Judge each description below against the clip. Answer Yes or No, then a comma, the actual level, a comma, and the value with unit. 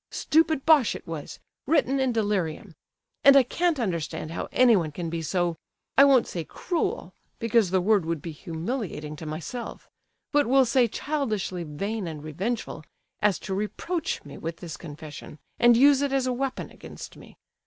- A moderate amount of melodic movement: No, wide, 8.1 semitones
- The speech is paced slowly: No, average, 165 wpm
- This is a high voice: Yes, high, 210 Hz